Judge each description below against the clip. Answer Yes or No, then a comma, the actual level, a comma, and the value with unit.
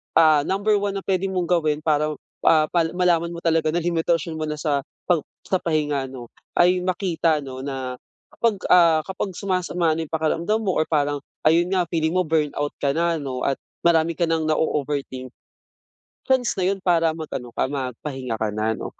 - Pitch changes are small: No, average, 3.3 semitones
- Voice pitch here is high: No, medium, 160 Hz